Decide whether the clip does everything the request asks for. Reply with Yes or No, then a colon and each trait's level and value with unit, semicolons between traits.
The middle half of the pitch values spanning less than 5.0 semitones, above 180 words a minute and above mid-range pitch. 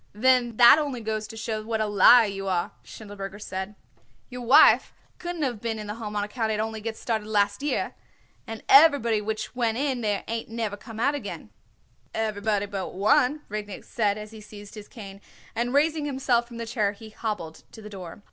Yes: narrow, 2.5 semitones; average, 200 wpm; high, 220 Hz